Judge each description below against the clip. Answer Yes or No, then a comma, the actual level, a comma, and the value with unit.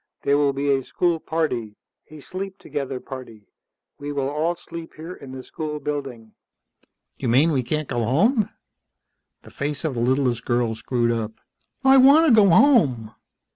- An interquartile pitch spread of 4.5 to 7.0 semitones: Yes, average, 5.0 semitones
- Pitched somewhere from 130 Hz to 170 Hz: Yes, medium, 140 Hz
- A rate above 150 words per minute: Yes, average, 170 wpm